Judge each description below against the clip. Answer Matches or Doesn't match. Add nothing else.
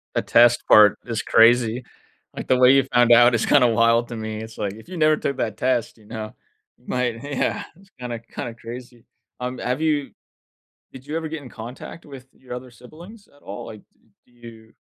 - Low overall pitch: Matches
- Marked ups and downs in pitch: Doesn't match